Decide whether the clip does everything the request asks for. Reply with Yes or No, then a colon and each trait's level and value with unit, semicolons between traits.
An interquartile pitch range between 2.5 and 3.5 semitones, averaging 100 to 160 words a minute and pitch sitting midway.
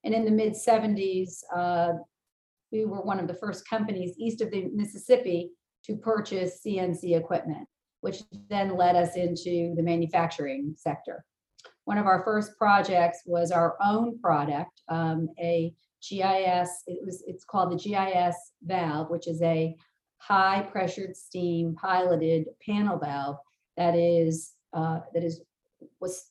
Yes: average, 2.9 semitones; average, 145 wpm; medium, 180 Hz